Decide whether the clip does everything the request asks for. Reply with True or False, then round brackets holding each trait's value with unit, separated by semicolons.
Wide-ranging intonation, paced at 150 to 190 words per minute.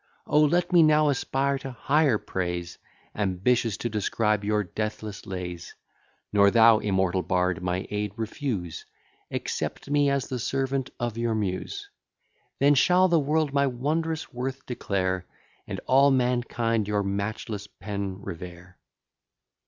False (5.9 semitones; 135 wpm)